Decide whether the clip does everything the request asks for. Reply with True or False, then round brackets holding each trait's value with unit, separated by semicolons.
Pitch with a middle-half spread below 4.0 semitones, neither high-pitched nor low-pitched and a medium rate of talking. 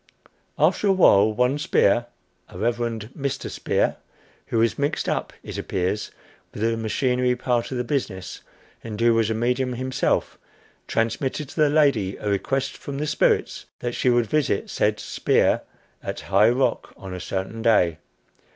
False (3.5 semitones; 120 Hz; 160 wpm)